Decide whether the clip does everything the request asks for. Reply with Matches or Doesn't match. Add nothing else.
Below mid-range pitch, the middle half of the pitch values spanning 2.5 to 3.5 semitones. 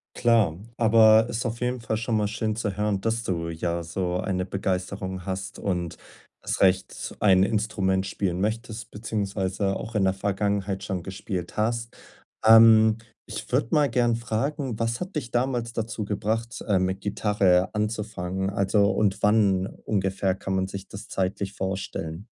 Matches